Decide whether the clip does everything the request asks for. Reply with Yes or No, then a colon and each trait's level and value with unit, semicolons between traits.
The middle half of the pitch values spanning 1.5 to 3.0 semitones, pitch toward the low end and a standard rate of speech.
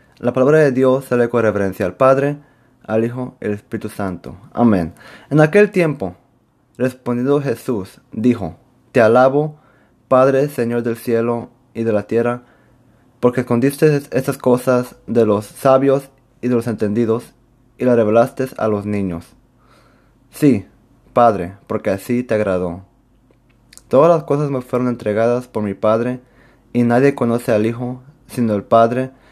Yes: average, 2.7 semitones; low, 120 Hz; average, 145 wpm